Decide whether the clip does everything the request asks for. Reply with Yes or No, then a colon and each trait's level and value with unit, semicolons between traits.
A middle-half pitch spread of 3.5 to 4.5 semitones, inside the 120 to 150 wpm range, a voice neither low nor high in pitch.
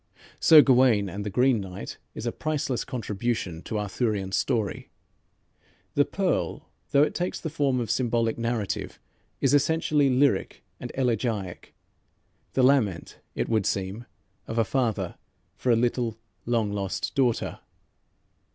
No: average, 4.1 semitones; slow, 135 wpm; low, 120 Hz